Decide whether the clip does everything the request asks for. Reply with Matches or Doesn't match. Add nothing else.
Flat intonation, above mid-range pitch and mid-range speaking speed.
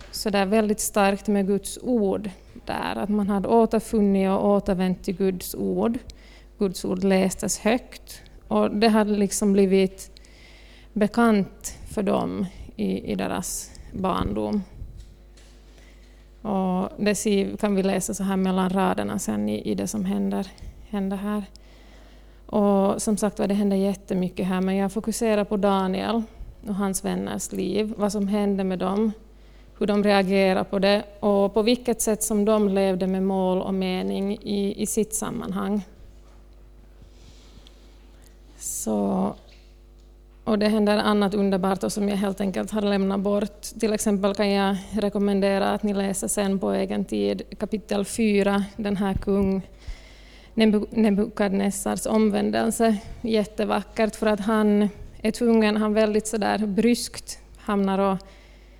Matches